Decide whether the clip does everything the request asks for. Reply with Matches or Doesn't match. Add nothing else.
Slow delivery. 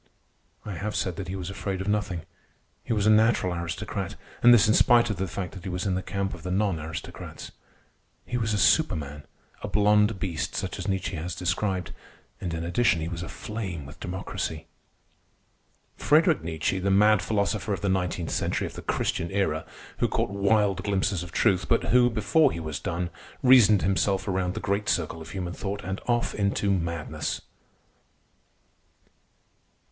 Doesn't match